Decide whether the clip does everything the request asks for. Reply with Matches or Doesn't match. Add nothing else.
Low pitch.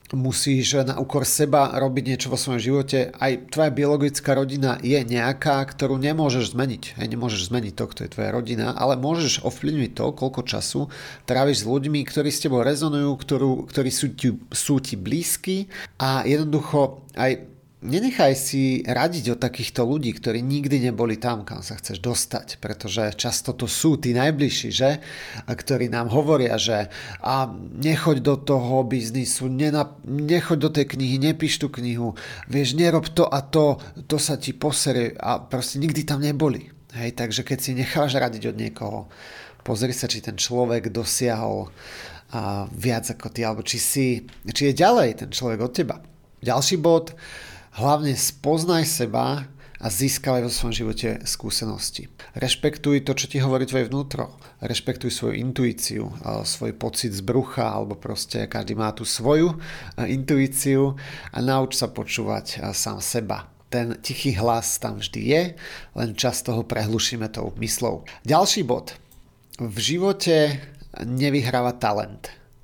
Matches